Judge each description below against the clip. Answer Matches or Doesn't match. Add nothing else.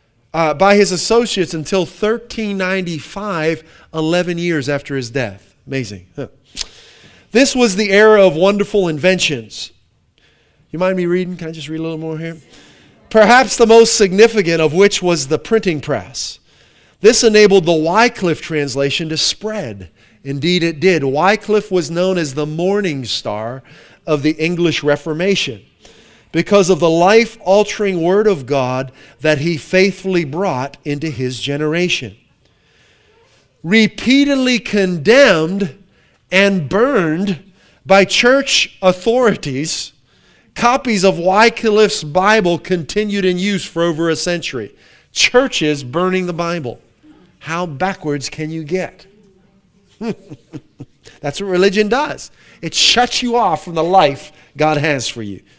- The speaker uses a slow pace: Matches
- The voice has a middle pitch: Matches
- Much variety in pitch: Doesn't match